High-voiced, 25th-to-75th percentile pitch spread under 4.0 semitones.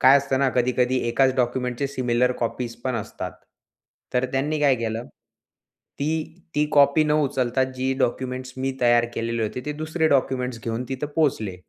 No: low, 130 Hz; narrow, 2.4 semitones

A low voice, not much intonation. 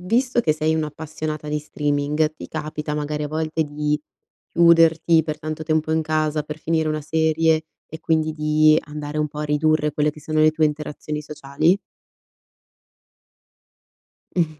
No: medium, 155 Hz; narrow, 0.9 semitones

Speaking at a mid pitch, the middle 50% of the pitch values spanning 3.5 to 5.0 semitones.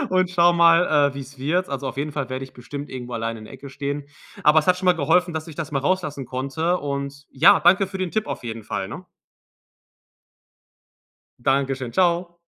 Yes: medium, 145 Hz; average, 4.4 semitones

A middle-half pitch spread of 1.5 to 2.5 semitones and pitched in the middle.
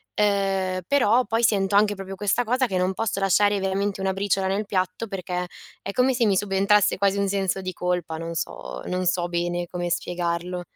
No: narrow, 2.2 semitones; high, 195 Hz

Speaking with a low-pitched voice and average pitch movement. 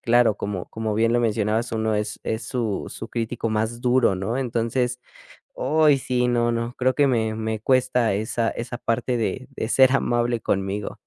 No: low, 115 Hz; narrow, 2.0 semitones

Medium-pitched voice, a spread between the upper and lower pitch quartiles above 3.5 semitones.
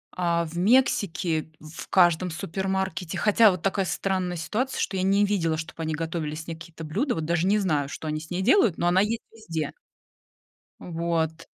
No: medium, 175 Hz; average, 3.1 semitones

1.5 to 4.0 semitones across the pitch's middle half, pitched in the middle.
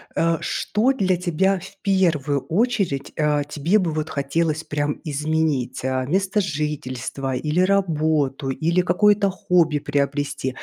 No: average, 4.4 semitones; medium, 155 Hz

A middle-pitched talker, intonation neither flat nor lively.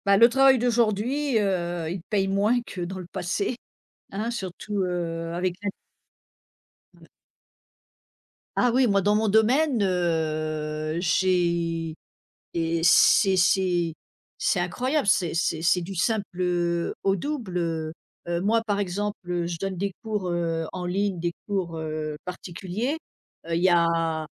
Yes: medium, 180 Hz; average, 3.5 semitones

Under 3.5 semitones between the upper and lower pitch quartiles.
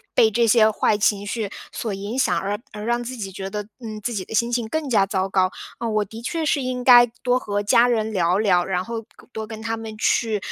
Yes: average, 2.8 semitones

